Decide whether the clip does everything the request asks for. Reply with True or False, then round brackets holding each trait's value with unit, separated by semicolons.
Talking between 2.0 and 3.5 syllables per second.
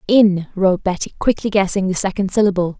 False (5.9 syllables/s)